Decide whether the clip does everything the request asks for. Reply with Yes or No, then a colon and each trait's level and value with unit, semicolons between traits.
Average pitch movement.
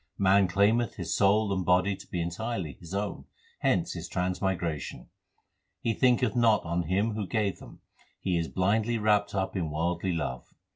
Yes: average, 3.3 semitones